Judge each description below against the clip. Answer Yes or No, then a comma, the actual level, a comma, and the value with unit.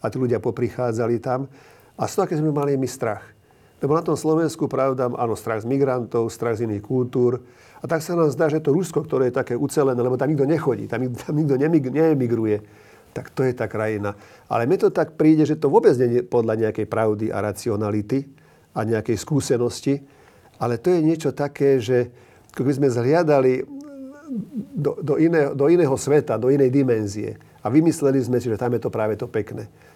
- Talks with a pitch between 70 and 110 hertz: No, low, 130 Hz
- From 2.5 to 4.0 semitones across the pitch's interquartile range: No, average, 4.4 semitones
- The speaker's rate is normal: No, fast, 200 wpm